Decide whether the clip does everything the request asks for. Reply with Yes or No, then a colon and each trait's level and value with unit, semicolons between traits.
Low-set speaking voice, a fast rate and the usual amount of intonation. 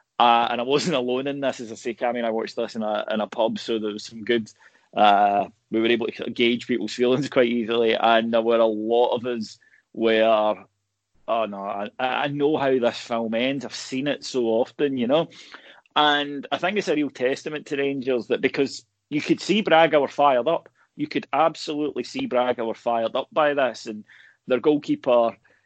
Yes: low, 120 Hz; fast, 210 wpm; average, 3.6 semitones